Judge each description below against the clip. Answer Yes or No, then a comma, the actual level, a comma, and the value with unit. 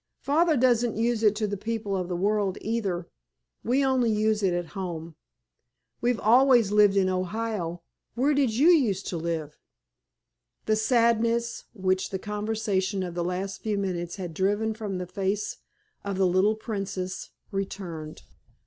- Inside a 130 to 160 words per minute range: Yes, average, 150 wpm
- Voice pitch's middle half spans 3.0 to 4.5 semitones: Yes, average, 3.4 semitones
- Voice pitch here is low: No, high, 205 Hz